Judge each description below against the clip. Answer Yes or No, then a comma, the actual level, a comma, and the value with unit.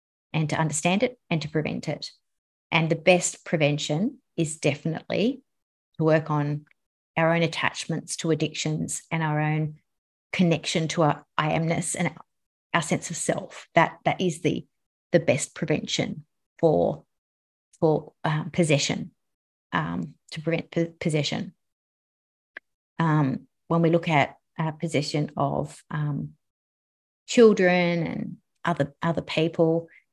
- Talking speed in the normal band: No, slow, 130 wpm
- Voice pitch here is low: No, medium, 160 Hz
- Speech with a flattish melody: Yes, narrow, 2.3 semitones